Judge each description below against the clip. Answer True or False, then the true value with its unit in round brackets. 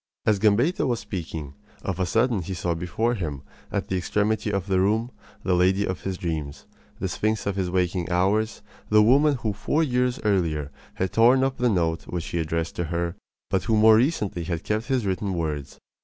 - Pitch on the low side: True (95 Hz)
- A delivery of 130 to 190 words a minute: False (200 wpm)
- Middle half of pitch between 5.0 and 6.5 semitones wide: False (4.4 semitones)